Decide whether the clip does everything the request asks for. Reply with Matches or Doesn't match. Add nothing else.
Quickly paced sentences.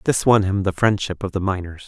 Matches